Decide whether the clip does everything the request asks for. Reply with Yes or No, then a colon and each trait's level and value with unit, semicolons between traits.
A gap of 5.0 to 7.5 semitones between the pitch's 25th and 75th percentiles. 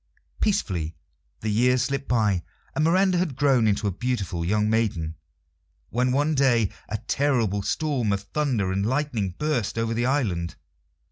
Yes: wide, 5.5 semitones